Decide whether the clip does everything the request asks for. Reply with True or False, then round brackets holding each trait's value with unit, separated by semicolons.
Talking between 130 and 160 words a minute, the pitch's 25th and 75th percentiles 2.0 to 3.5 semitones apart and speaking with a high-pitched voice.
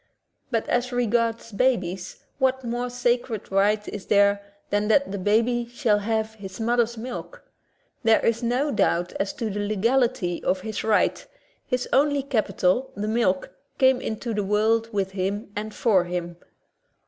True (155 wpm; 3.2 semitones; 220 Hz)